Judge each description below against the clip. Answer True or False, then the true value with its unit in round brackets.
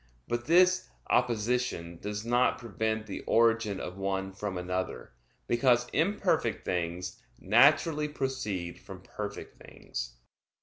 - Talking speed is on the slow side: True (115 wpm)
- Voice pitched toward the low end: True (110 Hz)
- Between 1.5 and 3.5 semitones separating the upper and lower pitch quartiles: False (5.1 semitones)